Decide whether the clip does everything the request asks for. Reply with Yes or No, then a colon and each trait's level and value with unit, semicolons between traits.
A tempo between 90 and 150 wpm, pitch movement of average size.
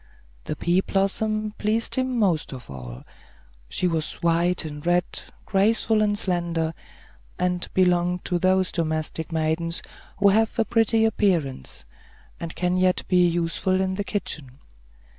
Yes: average, 140 wpm; average, 3.3 semitones